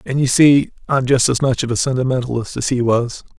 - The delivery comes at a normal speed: No, fast, 250 wpm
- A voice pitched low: Yes, low, 130 Hz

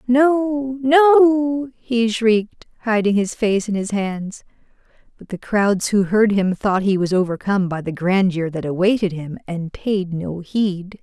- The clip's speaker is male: No, female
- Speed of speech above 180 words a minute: No, average, 165 wpm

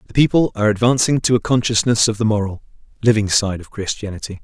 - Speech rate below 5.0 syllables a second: No, 6.5 syllables/s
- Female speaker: No, male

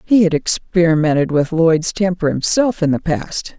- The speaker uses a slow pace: No, average, 165 wpm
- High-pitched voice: No, medium, 165 Hz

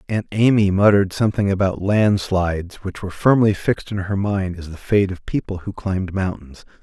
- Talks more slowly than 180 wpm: No, average, 185 wpm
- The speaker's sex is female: No, male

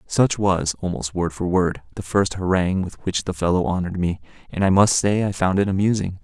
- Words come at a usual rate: No, fast, 220 wpm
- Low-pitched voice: Yes, very low, 95 Hz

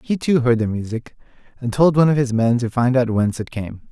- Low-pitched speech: Yes, low, 125 Hz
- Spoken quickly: Yes, fast, 260 wpm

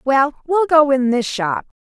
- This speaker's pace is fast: No, average, 195 wpm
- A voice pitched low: No, very high, 275 Hz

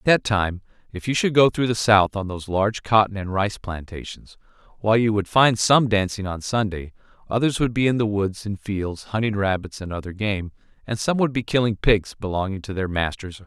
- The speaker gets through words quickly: Yes, fast, 225 wpm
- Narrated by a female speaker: No, male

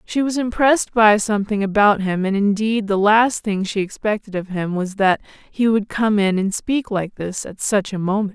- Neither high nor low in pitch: No, high, 205 Hz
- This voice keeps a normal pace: No, fast, 215 wpm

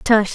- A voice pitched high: Yes, high, 215 Hz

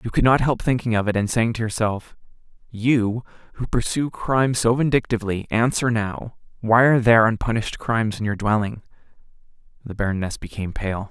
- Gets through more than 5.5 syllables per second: Yes, 5.7 syllables/s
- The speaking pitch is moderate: No, low, 110 Hz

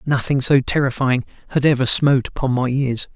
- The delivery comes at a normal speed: Yes, average, 170 wpm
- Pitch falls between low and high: No, low, 130 Hz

